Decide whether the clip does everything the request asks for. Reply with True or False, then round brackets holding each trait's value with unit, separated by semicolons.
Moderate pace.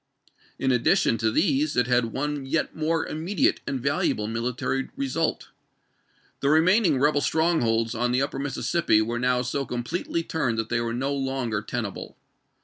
True (160 wpm)